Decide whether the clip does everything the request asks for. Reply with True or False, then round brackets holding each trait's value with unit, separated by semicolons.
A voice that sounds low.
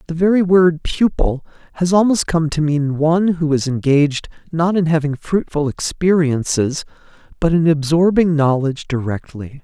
False (160 Hz)